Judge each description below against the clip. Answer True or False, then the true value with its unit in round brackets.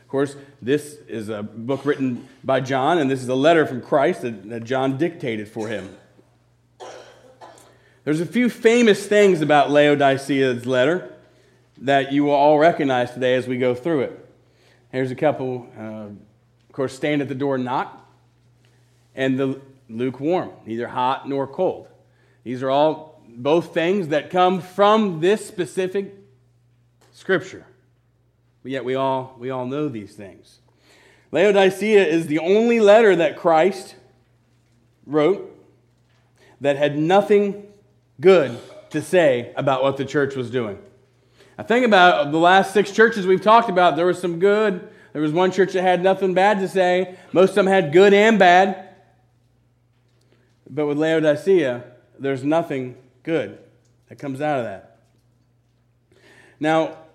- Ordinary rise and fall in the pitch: False (6.5 semitones)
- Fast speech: False (145 wpm)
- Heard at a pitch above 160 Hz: False (135 Hz)